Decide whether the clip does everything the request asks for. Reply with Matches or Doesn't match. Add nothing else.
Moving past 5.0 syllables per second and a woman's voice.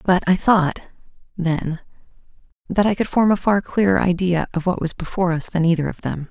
Matches